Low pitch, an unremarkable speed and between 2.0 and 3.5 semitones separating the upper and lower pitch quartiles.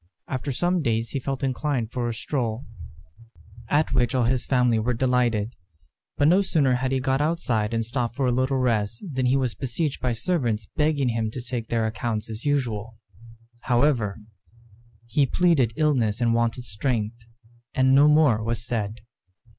Yes: low, 125 Hz; average, 170 wpm; average, 3.1 semitones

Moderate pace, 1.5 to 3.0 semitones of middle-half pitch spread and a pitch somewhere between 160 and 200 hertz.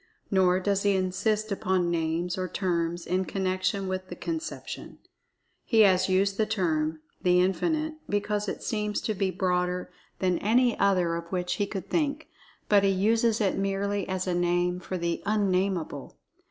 Yes: average, 165 wpm; narrow, 2.4 semitones; high, 190 Hz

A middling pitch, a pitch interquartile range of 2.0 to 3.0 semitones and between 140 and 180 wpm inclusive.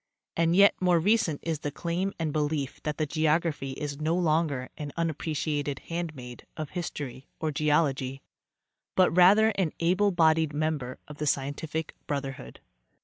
Yes: medium, 155 Hz; average, 2.7 semitones; average, 145 wpm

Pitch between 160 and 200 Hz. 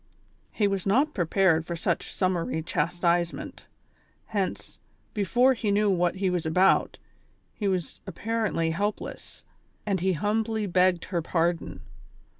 Yes: medium, 185 Hz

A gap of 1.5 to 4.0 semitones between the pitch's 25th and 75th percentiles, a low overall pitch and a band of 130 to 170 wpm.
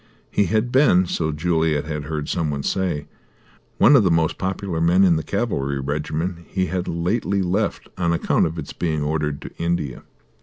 No: average, 3.5 semitones; very low, 85 Hz; average, 185 wpm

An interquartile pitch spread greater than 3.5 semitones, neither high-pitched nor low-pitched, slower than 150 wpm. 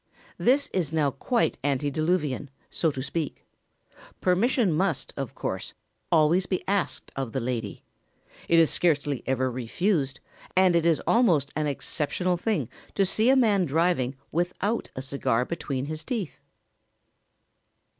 Yes: average, 5.1 semitones; medium, 160 Hz; slow, 135 wpm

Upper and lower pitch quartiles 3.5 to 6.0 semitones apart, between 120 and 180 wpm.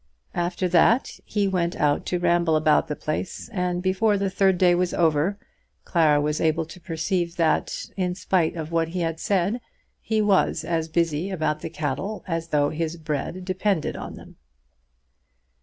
No: average, 2.8 semitones; average, 170 wpm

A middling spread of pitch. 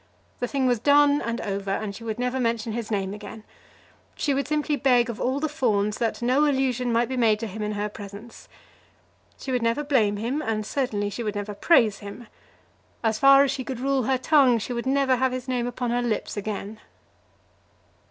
Yes: average, 3.7 semitones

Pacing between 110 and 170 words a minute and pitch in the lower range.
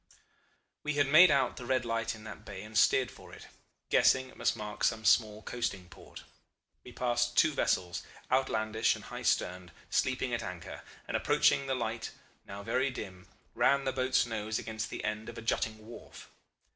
No: average, 185 wpm; low, 115 Hz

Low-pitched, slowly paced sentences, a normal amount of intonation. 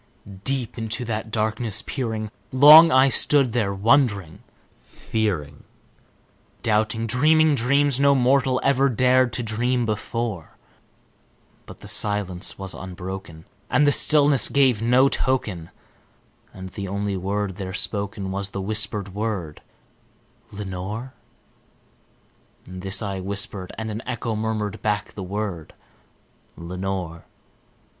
Yes: low, 110 Hz; slow, 115 wpm; average, 4.5 semitones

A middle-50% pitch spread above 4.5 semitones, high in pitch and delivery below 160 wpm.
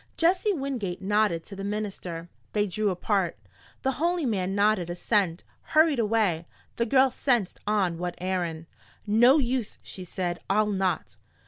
Yes: average, 4.9 semitones; high, 205 Hz; average, 145 wpm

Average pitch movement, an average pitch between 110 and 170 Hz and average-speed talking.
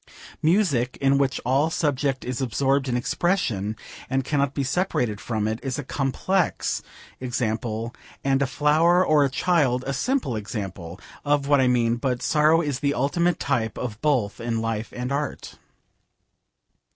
Yes: average, 3.7 semitones; low, 135 Hz; average, 150 wpm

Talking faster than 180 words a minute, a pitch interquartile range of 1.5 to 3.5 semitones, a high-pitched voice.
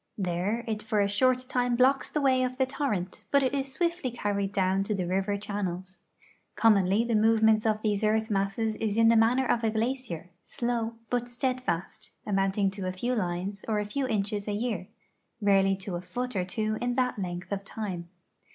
No: average, 200 wpm; average, 3.9 semitones; high, 215 Hz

